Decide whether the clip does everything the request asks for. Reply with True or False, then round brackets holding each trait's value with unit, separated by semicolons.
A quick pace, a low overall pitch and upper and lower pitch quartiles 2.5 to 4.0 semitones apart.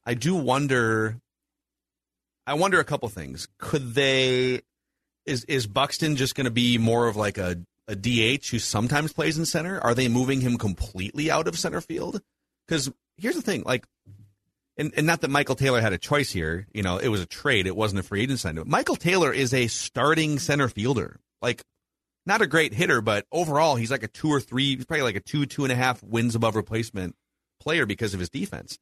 False (210 wpm; 125 Hz; 4.5 semitones)